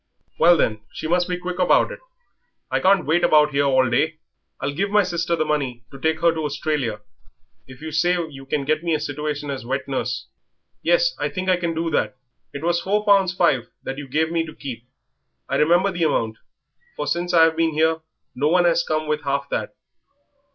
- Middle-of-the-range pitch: Yes, medium, 160 Hz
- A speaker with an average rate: No, fast, 210 wpm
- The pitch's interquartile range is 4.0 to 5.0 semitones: No, average, 3.6 semitones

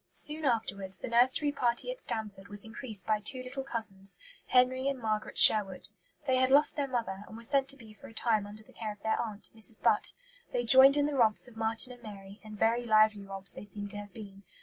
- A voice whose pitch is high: Yes, high, 225 Hz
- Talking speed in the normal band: No, fast, 230 wpm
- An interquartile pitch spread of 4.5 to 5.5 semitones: No, average, 3.7 semitones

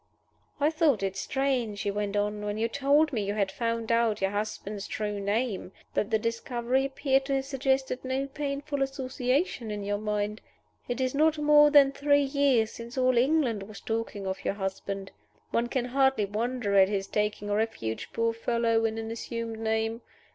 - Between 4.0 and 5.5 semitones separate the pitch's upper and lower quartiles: Yes, average, 4.4 semitones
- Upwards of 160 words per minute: Yes, average, 180 wpm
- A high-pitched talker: Yes, high, 230 Hz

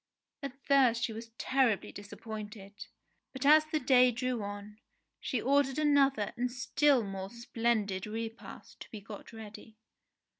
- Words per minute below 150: Yes, average, 140 wpm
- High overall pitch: Yes, high, 235 Hz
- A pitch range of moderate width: Yes, average, 3.9 semitones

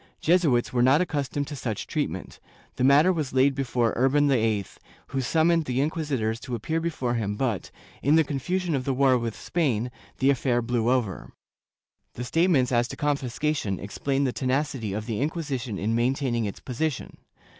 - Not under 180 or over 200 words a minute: No, average, 170 wpm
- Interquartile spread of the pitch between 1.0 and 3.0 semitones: No, average, 3.7 semitones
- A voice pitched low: Yes, low, 130 Hz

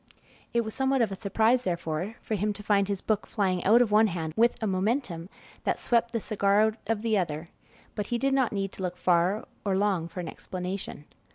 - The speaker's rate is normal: No, fast, 220 wpm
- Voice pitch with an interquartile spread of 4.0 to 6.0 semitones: No, average, 3.5 semitones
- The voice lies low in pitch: No, high, 205 Hz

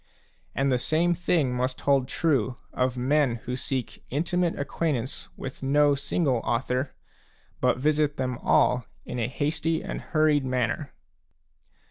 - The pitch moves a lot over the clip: No, average, 3.3 semitones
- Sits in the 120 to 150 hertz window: Yes, low, 135 Hz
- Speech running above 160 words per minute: No, average, 140 wpm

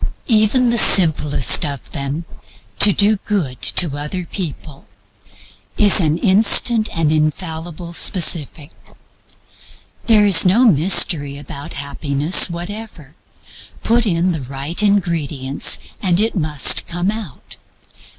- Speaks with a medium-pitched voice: Yes, medium, 170 Hz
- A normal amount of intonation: No, wide, 5.7 semitones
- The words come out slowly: Yes, slow, 110 wpm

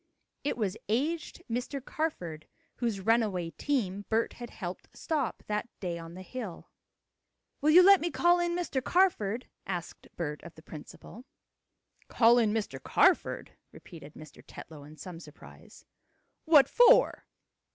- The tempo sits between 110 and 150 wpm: Yes, average, 140 wpm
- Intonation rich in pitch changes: Yes, wide, 8.7 semitones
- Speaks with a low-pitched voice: No, high, 225 Hz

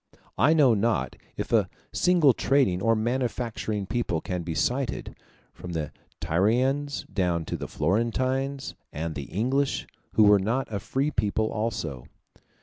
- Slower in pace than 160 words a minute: Yes, average, 145 wpm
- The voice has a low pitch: Yes, low, 110 Hz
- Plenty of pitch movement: Yes, wide, 6.2 semitones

